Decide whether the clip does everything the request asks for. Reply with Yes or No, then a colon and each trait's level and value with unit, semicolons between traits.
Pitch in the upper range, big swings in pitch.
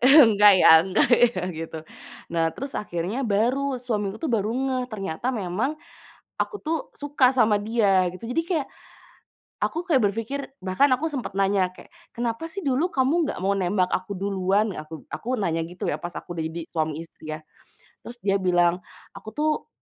Yes: high, 210 Hz; wide, 6.3 semitones